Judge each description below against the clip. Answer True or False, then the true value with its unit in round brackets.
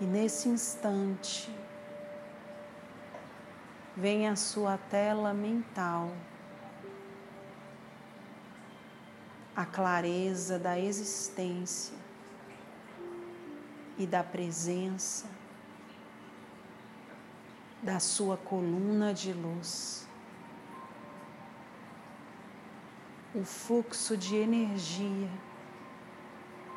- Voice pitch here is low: False (195 Hz)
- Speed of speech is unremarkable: False (55 wpm)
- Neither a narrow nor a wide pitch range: False (1.9 semitones)